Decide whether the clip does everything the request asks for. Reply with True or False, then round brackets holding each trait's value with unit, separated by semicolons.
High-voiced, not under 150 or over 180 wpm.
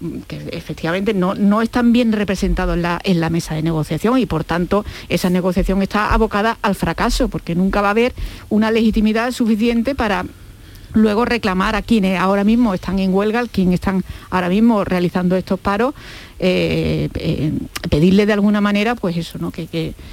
True (195 Hz; 175 wpm)